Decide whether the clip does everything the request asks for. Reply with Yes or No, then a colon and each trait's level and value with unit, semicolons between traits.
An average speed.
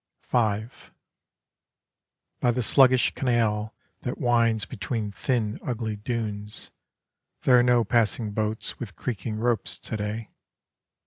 No: slow, 115 wpm